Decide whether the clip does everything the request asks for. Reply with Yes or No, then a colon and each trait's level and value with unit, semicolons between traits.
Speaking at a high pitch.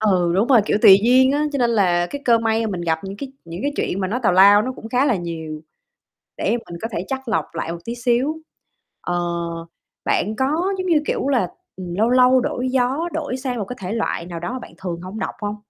Yes: high, 225 Hz